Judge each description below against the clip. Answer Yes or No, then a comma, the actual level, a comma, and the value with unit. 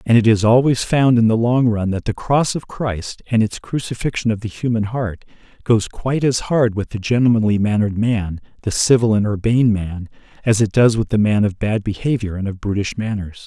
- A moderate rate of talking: No, fast, 215 wpm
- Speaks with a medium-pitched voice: No, low, 110 Hz